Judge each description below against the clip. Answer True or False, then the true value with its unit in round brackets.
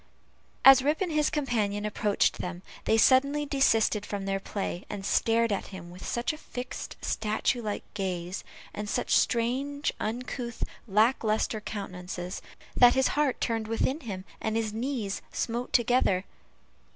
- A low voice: False (225 Hz)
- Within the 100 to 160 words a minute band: True (150 wpm)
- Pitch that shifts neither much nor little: True (4.1 semitones)